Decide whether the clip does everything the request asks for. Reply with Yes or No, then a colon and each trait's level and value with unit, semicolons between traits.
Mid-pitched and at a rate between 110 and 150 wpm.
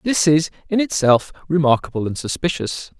Yes: medium, 155 Hz; average, 140 wpm